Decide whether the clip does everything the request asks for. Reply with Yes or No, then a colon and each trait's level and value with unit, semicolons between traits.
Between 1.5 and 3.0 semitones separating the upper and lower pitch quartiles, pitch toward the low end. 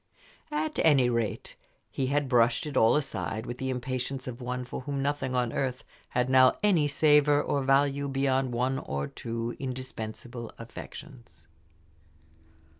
Yes: narrow, 2.5 semitones; low, 130 Hz